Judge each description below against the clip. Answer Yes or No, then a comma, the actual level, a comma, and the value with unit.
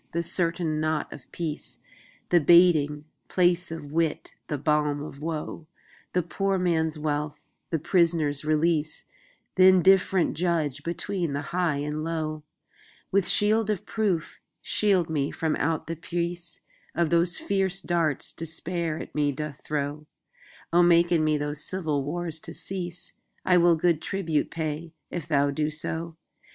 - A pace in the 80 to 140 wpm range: Yes, slow, 135 wpm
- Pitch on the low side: No, medium, 165 Hz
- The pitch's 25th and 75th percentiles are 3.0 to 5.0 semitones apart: No, narrow, 2.6 semitones